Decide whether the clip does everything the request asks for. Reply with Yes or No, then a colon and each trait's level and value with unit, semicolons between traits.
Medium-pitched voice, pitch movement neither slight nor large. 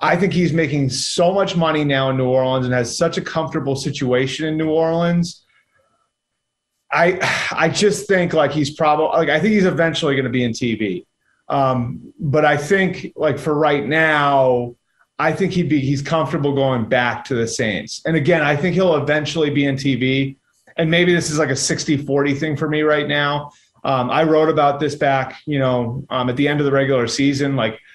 Yes: medium, 150 Hz; average, 3.1 semitones